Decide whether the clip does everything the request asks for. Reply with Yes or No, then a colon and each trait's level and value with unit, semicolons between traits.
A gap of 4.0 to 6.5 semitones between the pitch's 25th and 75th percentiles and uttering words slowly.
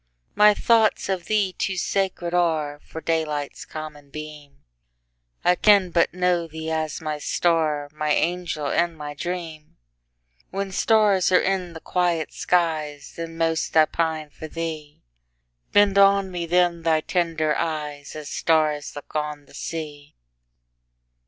No: average, 3.2 semitones; slow, 120 wpm